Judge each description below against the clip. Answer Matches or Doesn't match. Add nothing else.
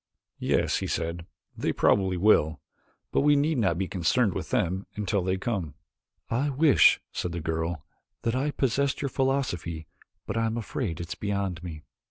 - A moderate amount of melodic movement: Doesn't match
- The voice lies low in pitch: Matches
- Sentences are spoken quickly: Doesn't match